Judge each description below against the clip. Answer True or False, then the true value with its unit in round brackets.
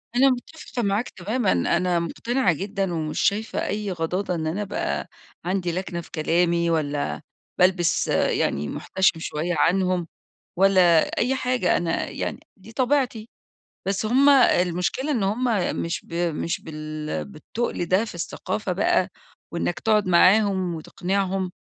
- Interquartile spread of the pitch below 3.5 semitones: False (3.9 semitones)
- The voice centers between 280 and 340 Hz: False (185 Hz)